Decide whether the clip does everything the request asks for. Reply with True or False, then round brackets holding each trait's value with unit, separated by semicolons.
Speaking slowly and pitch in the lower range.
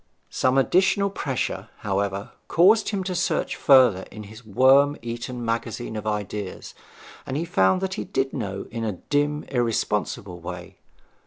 False (150 wpm; 120 Hz)